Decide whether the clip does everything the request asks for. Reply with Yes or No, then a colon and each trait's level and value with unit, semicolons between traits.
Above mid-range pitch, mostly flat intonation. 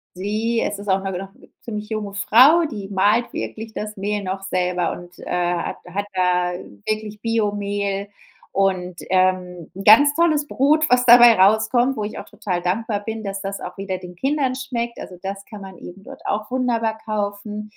No: high, 205 Hz; average, 3.0 semitones